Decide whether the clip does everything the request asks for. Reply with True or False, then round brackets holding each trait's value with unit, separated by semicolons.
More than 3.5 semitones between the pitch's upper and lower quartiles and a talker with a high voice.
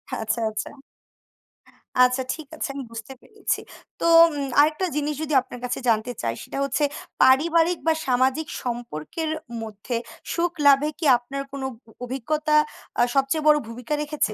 True (4.1 semitones; 275 Hz)